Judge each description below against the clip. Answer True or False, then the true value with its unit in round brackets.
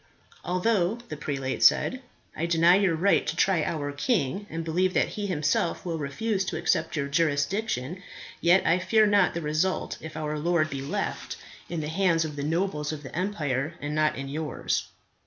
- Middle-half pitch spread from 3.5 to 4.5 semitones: True (3.8 semitones)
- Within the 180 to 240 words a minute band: True (185 wpm)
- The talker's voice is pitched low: False (165 Hz)